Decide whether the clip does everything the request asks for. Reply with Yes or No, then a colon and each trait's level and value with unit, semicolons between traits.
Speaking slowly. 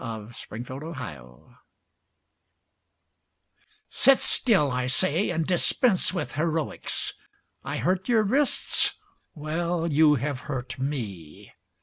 Yes: slow, 100 wpm